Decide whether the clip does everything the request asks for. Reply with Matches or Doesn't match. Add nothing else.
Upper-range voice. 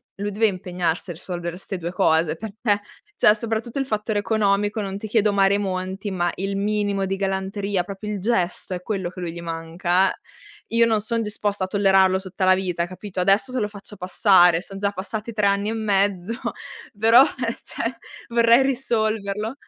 Matches